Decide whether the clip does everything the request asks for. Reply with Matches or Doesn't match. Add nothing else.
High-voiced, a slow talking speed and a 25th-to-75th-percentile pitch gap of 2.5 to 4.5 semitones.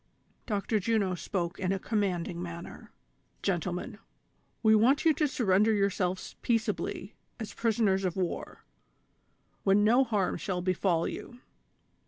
Matches